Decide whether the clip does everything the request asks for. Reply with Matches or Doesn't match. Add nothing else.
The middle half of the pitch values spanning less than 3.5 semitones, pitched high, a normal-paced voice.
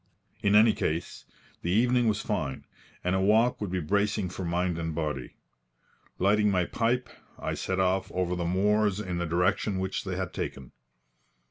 Doesn't match